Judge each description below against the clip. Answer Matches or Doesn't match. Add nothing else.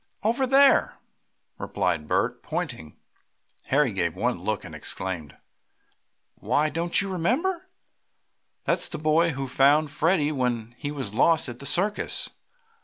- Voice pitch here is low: Doesn't match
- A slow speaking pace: Matches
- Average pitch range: Doesn't match